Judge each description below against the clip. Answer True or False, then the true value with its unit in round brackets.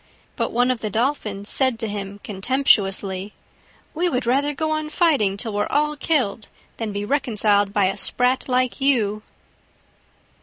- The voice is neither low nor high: False (230 Hz)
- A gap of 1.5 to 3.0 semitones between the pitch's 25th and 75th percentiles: False (5.2 semitones)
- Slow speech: False (155 wpm)